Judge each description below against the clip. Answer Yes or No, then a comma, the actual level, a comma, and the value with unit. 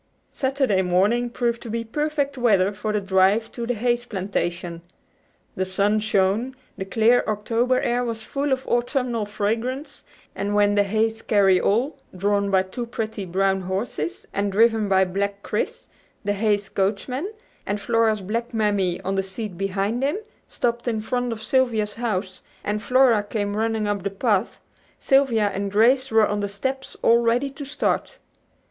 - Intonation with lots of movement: No, average, 3.3 semitones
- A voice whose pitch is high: Yes, high, 215 Hz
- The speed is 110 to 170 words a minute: Yes, average, 165 wpm